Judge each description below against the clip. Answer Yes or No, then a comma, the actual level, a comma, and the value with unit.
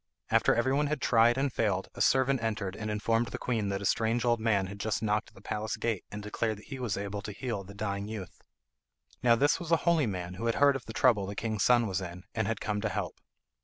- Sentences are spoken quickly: Yes, fast, 255 wpm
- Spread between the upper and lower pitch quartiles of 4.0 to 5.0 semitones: No, average, 2.9 semitones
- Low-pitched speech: Yes, low, 110 Hz